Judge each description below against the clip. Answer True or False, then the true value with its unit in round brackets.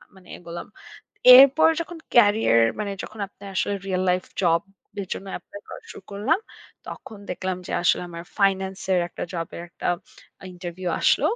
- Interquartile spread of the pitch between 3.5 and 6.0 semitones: False (2.6 semitones)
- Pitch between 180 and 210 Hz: True (190 Hz)